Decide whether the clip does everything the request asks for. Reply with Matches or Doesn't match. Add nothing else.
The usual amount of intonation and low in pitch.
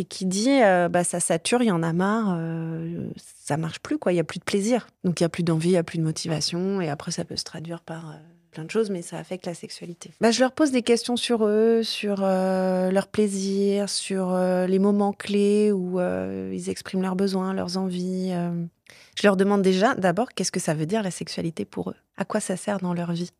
Doesn't match